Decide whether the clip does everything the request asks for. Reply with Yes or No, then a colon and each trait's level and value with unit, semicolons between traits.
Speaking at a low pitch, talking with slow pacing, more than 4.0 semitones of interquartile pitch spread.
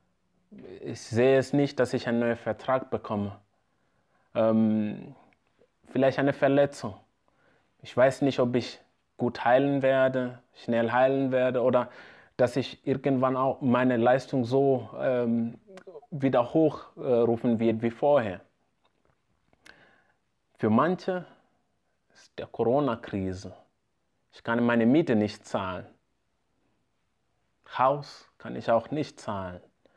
No: low, 125 Hz; slow, 115 wpm; average, 2.7 semitones